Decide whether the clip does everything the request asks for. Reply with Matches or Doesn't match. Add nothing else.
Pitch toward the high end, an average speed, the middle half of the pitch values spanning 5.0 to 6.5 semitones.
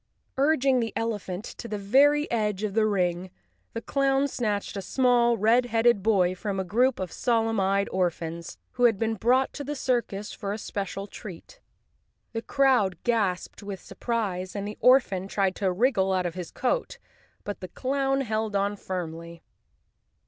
Doesn't match